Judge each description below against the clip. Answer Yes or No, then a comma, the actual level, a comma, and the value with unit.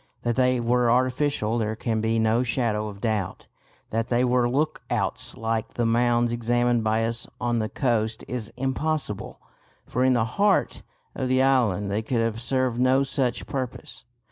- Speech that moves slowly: No, average, 170 wpm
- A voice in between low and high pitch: No, low, 120 Hz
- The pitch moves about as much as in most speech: No, narrow, 2.3 semitones